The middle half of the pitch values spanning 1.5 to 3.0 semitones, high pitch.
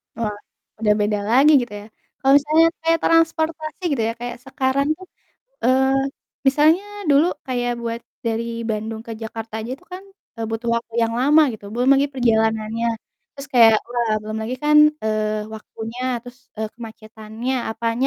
No: average, 3.8 semitones; high, 235 Hz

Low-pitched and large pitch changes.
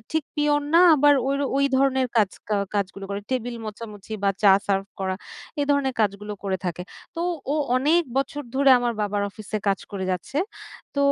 No: high, 225 Hz; wide, 5.7 semitones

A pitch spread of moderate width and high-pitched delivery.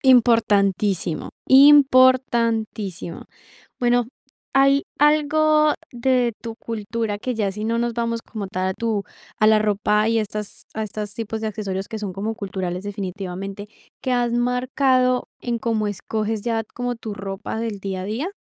Yes: average, 3.2 semitones; high, 220 Hz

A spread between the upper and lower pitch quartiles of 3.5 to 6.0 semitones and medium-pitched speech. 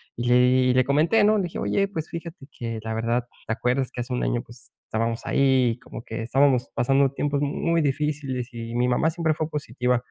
No: average, 3.8 semitones; low, 130 Hz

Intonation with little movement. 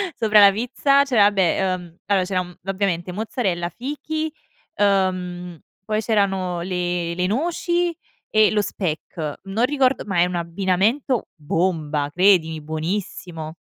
No: average, 3.8 semitones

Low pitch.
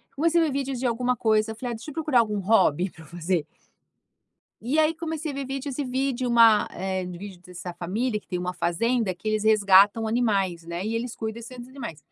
No: high, 225 Hz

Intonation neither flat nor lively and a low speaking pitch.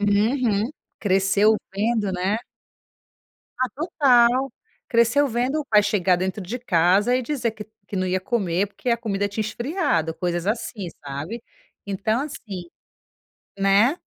No: average, 3.9 semitones; high, 210 Hz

